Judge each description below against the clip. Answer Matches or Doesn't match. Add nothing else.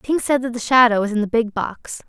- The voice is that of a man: Doesn't match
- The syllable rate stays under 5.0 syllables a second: Doesn't match